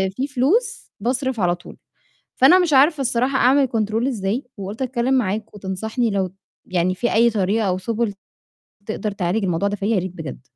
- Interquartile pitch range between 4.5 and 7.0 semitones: Yes, average, 4.9 semitones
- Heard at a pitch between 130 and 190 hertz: No, high, 220 Hz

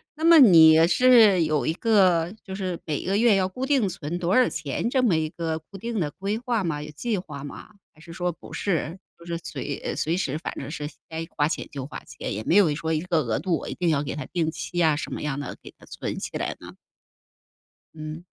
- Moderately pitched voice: Yes, medium, 170 Hz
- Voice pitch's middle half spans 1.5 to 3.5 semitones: No, average, 4.2 semitones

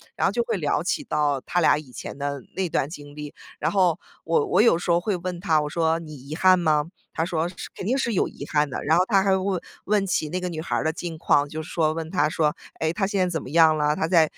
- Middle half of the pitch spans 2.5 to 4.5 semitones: Yes, average, 3.4 semitones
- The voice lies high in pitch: No, medium, 165 Hz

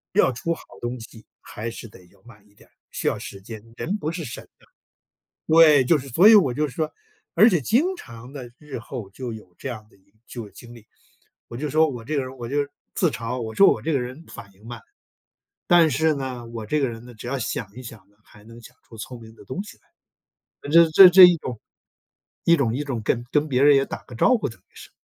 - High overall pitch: No, low, 125 Hz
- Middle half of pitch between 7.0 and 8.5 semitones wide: No, average, 5.1 semitones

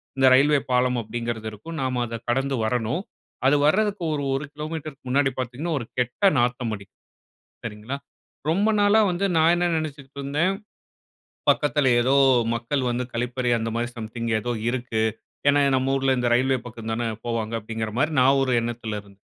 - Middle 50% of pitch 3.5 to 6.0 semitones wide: Yes, average, 3.8 semitones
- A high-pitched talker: No, low, 130 Hz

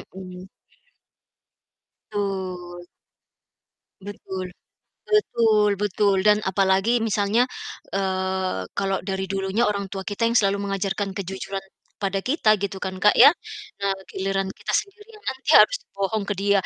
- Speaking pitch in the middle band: No, high, 195 Hz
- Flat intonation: Yes, narrow, 1.8 semitones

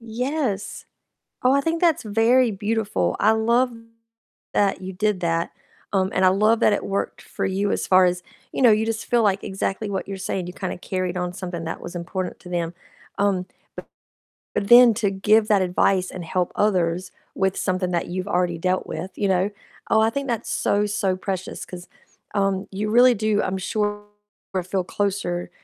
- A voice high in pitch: Yes, high, 195 Hz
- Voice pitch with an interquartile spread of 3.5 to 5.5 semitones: No, average, 2.9 semitones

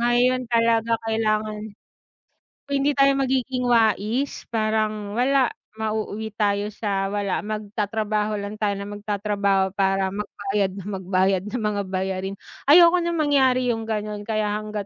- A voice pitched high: Yes, high, 215 Hz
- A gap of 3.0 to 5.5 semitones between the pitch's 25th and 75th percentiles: No, narrow, 2.6 semitones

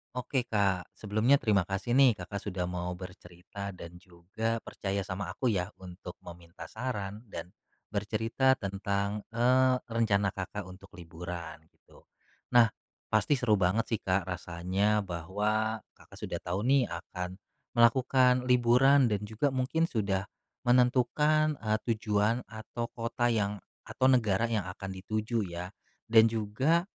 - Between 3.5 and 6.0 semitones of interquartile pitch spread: Yes, average, 4.2 semitones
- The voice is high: No, low, 105 Hz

